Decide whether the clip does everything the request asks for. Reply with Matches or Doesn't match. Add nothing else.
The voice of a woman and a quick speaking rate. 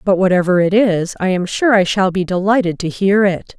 Matches